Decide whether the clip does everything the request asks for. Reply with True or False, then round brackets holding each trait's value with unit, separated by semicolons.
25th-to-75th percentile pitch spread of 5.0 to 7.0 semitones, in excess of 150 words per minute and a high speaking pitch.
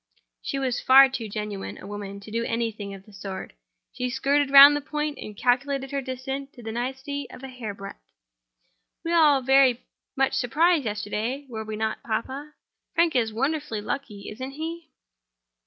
False (4.3 semitones; 170 wpm; 260 Hz)